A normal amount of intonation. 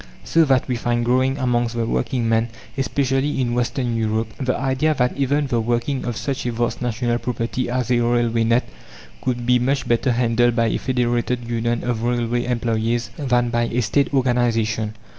No: narrow, 1.5 semitones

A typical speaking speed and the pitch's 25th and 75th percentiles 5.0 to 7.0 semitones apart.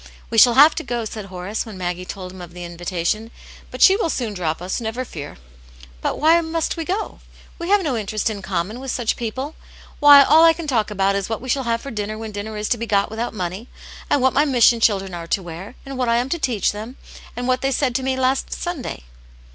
No: fast, 255 wpm; average, 5.3 semitones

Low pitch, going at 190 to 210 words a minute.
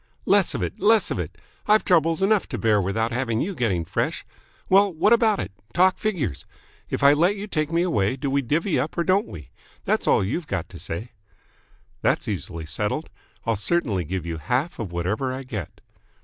Yes: low, 130 Hz; average, 200 wpm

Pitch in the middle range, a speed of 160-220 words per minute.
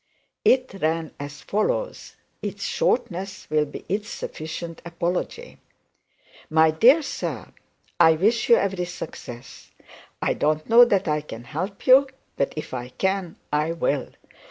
No: medium, 170 Hz; slow, 135 wpm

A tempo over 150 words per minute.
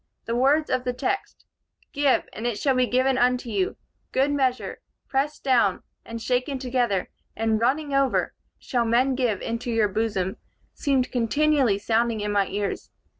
Yes: average, 160 wpm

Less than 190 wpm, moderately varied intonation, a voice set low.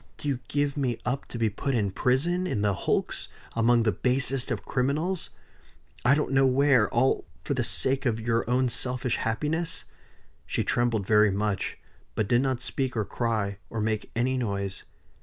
Yes: average, 175 wpm; average, 3.6 semitones; low, 120 Hz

